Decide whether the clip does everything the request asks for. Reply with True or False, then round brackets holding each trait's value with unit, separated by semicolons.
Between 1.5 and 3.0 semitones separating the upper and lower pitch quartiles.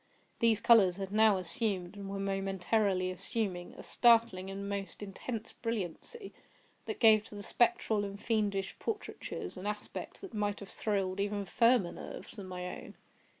True (2.5 semitones)